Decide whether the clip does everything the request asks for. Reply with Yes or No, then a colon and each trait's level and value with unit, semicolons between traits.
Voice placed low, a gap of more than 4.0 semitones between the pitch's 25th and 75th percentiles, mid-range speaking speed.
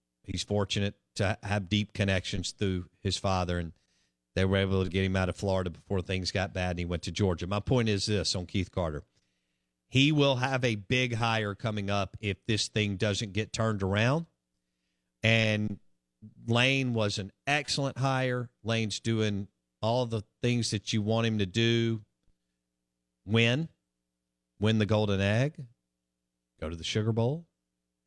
Yes: low, 100 Hz; average, 4.5 semitones; average, 165 wpm